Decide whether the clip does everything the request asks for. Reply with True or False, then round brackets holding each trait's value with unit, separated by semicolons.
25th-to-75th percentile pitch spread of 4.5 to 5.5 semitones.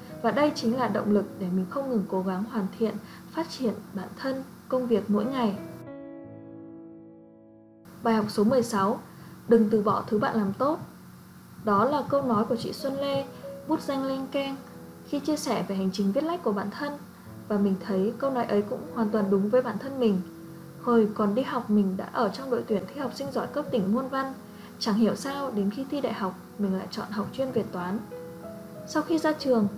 True (5.1 semitones)